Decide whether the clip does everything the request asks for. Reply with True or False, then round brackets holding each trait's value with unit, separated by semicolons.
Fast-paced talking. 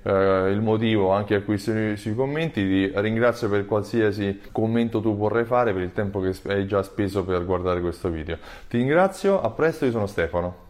True (185 wpm)